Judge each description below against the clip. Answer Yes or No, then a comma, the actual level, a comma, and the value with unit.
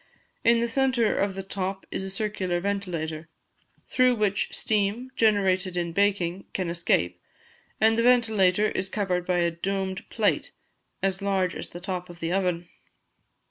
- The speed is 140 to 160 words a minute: Yes, average, 155 wpm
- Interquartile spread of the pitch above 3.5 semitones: No, average, 2.9 semitones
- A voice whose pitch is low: No, high, 190 Hz